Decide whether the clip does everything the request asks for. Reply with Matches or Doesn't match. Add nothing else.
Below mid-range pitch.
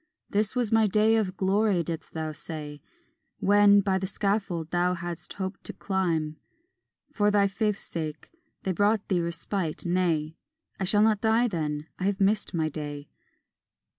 Doesn't match